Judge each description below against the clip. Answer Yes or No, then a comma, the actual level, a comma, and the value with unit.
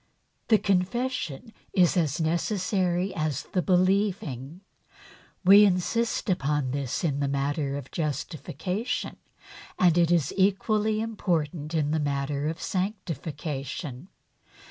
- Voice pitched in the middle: Yes, medium, 170 Hz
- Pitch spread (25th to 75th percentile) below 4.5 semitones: No, average, 5.0 semitones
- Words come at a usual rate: No, slow, 110 wpm